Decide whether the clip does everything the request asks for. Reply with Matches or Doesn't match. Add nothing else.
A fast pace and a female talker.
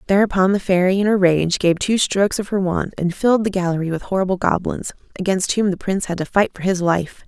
Matches